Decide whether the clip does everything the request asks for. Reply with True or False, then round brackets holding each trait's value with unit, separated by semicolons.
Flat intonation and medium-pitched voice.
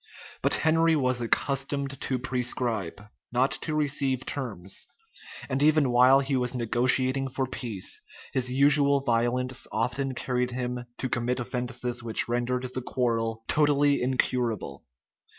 False (2.1 semitones; 125 Hz)